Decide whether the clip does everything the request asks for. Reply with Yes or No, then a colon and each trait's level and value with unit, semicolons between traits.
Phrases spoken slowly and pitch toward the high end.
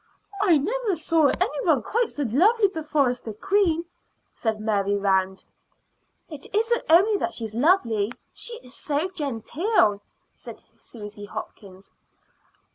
Yes: slow, 130 wpm; very high, 290 Hz